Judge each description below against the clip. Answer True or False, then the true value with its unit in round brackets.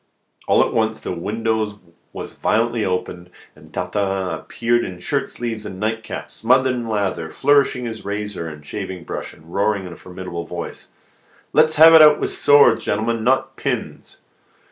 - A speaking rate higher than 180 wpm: False (165 wpm)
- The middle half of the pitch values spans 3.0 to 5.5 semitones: True (4.2 semitones)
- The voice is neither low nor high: False (105 Hz)